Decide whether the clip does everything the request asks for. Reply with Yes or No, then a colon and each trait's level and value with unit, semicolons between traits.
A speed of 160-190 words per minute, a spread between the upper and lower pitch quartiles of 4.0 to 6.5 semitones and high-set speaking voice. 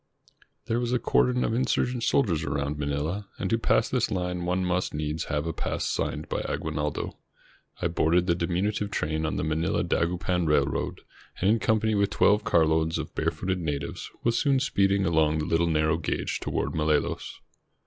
No: average, 175 wpm; average, 4.6 semitones; very low, 85 Hz